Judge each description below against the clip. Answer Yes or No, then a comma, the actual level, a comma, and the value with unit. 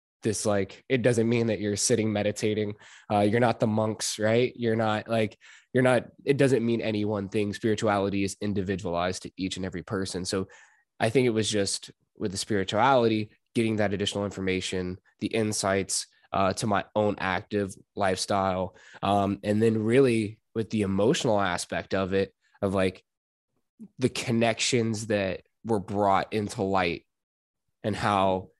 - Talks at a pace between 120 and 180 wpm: Yes, average, 160 wpm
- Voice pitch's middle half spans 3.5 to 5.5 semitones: No, narrow, 2.6 semitones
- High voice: No, low, 105 Hz